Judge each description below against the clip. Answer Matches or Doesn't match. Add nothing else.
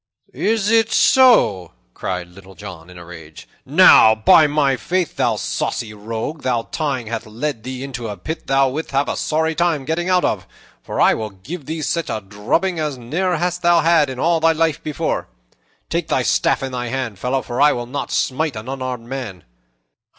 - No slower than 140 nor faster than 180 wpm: Doesn't match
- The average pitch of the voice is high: Doesn't match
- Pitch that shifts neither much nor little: Doesn't match